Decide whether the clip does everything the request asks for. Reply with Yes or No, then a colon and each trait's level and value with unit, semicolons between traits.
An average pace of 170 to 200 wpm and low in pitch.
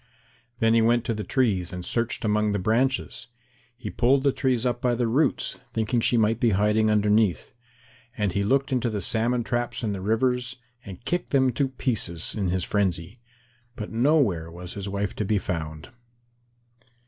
Yes: average, 180 wpm; low, 110 Hz